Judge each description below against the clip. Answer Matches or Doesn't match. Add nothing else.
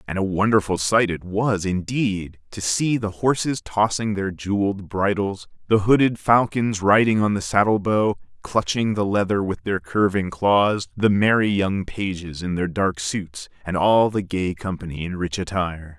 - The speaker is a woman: Doesn't match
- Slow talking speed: Doesn't match